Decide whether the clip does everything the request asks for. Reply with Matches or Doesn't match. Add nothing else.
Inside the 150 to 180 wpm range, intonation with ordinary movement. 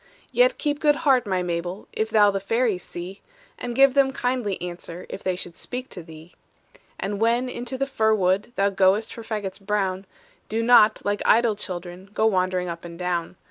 Doesn't match